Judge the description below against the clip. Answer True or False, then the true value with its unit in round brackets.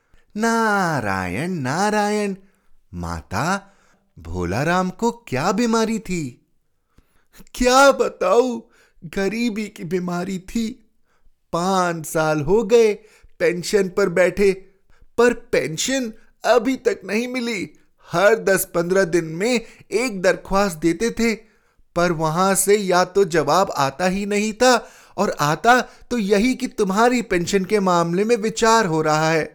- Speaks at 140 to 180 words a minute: False (125 wpm)